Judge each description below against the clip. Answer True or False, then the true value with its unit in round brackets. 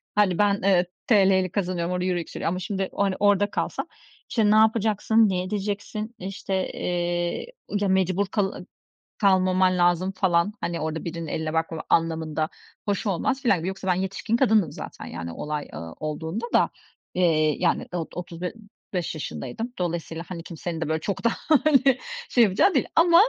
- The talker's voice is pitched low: False (185 Hz)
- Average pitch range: True (3.4 semitones)